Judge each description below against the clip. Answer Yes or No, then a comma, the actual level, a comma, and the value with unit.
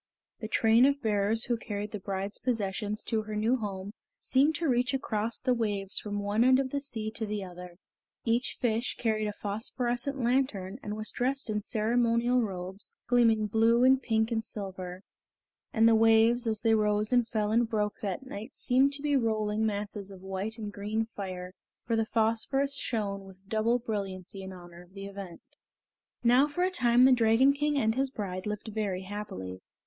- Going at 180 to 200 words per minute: Yes, average, 185 wpm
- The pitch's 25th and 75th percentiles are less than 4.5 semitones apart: Yes, average, 3.1 semitones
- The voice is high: Yes, high, 220 Hz